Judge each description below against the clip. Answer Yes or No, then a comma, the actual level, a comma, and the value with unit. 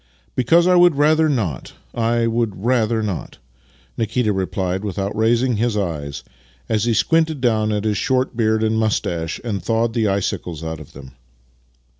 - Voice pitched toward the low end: Yes, low, 110 Hz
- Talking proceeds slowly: No, average, 165 wpm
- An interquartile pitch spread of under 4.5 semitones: Yes, average, 3.7 semitones